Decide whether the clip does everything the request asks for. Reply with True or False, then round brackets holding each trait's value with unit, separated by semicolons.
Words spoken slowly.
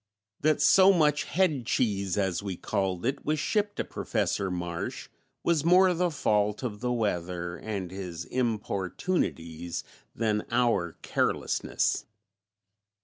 True (125 wpm)